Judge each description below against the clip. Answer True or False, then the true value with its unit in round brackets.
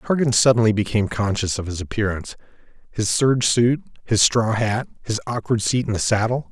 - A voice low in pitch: True (110 Hz)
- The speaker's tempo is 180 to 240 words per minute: False (165 wpm)